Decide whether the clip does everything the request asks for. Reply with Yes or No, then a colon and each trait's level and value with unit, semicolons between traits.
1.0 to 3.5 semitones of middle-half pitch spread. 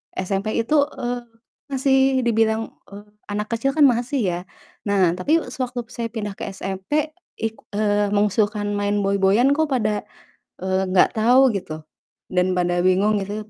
No: average, 4.0 semitones